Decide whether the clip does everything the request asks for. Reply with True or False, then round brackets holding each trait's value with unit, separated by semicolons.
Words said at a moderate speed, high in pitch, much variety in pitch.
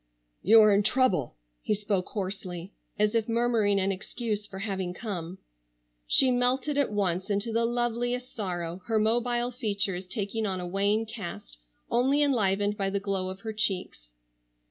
False (160 wpm; 205 Hz; 3.4 semitones)